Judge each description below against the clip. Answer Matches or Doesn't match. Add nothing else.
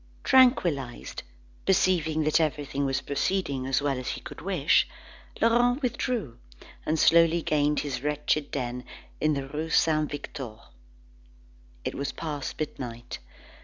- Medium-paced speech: Doesn't match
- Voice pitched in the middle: Matches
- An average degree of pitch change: Matches